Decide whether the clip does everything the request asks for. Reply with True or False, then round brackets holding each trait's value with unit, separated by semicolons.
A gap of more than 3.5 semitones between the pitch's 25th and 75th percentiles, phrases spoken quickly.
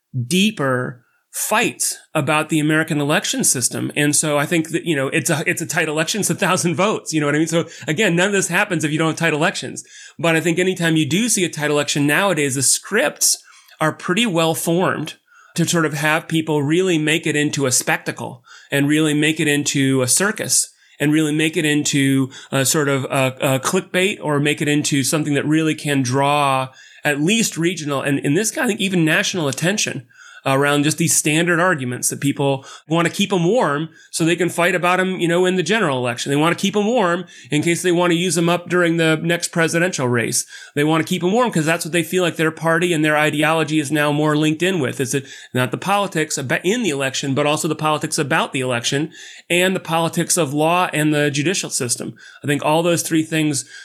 False (2.9 semitones; 225 wpm)